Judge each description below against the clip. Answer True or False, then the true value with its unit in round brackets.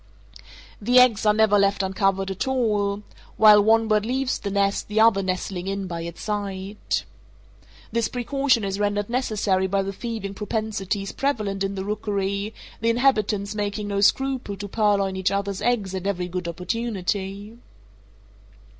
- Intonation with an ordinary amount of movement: False (2.1 semitones)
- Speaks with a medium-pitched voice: False (205 Hz)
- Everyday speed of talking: True (150 wpm)